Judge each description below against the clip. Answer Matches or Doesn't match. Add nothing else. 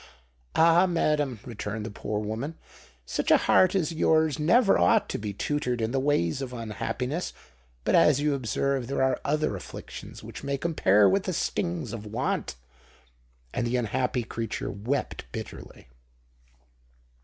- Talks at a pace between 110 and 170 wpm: Matches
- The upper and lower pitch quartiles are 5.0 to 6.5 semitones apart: Matches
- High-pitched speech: Doesn't match